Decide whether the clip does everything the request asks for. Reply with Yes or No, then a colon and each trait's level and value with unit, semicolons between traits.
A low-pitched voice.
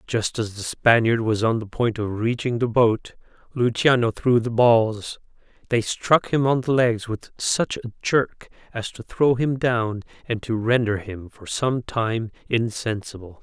Yes: low, 115 Hz